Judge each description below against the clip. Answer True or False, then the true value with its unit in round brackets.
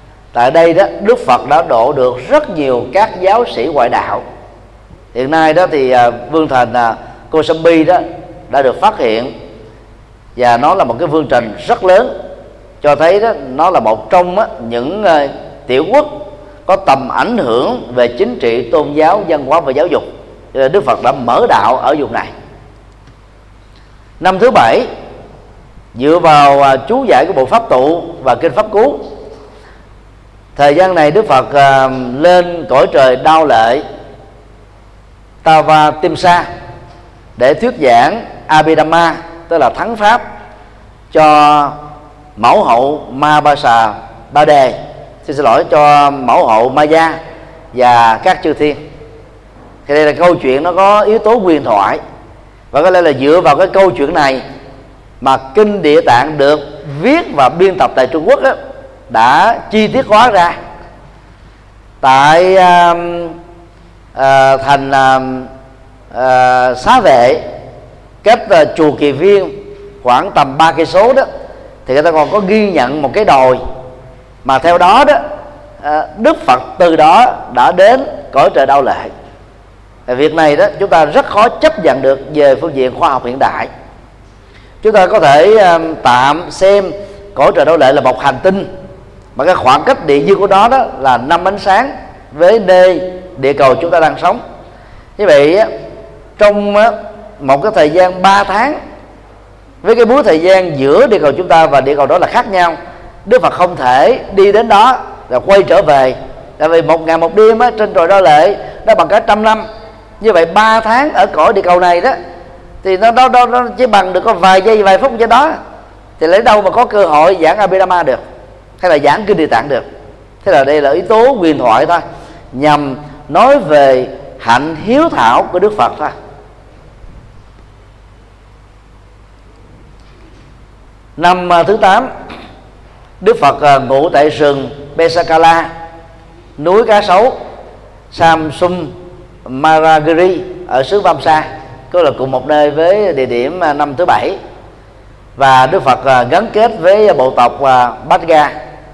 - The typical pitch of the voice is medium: True (150 Hz)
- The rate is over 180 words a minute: False (165 wpm)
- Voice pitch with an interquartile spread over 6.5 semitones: True (6.9 semitones)